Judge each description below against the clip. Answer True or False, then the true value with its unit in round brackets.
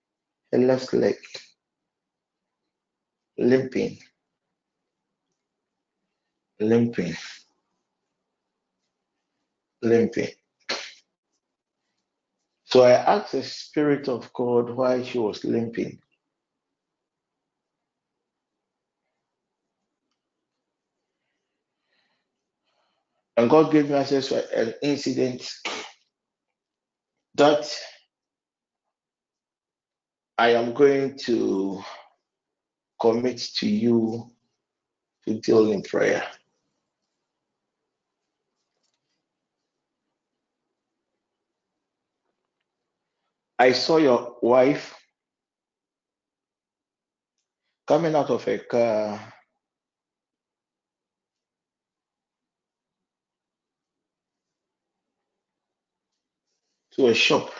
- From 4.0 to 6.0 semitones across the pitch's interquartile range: False (3.0 semitones)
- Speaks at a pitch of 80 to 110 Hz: False (125 Hz)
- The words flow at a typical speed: False (50 wpm)